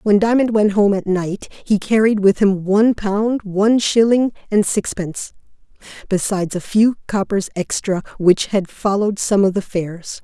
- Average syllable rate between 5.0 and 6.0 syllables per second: No, 4.8 syllables/s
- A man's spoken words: No, female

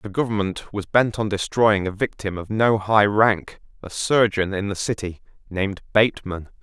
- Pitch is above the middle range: No, low, 100 Hz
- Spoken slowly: No, average, 170 wpm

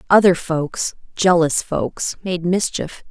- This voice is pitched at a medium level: Yes, medium, 170 Hz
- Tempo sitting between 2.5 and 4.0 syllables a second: Yes, 3.5 syllables/s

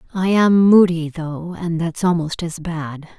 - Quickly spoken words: No, average, 170 wpm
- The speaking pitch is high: No, medium, 170 Hz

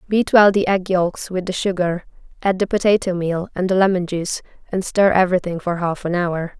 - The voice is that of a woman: Yes, female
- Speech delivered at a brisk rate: Yes, fast, 210 wpm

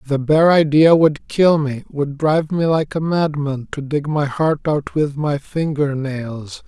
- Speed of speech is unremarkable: Yes, average, 180 wpm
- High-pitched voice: No, medium, 150 Hz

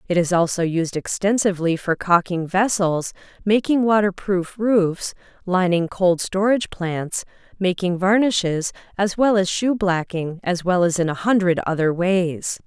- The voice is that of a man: No, female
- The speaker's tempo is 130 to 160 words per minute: Yes, average, 140 wpm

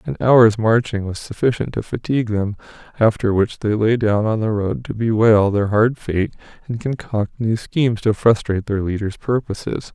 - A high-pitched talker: No, low, 110 Hz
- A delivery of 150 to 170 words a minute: No, average, 180 wpm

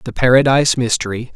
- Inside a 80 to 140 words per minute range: Yes, slow, 135 wpm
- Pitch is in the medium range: No, low, 125 Hz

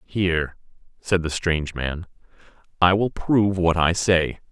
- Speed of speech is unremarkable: Yes, average, 145 wpm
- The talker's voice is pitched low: Yes, very low, 90 Hz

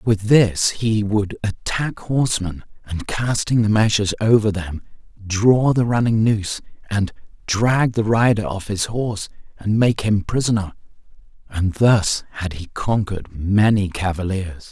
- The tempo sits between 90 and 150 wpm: Yes, average, 140 wpm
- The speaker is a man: Yes, male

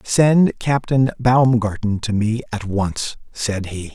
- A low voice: Yes, low, 115 Hz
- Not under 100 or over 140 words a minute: Yes, slow, 135 wpm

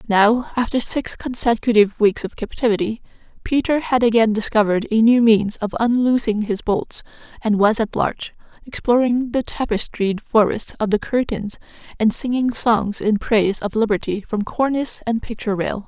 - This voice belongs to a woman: Yes, female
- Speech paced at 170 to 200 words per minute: No, average, 155 wpm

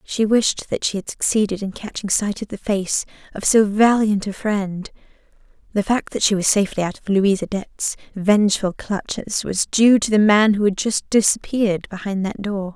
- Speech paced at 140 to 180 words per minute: No, average, 195 wpm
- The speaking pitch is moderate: No, high, 205 Hz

